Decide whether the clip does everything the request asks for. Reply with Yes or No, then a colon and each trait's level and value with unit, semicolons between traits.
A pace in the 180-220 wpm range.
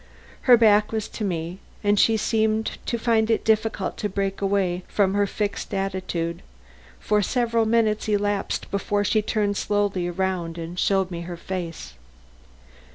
No: average, 155 wpm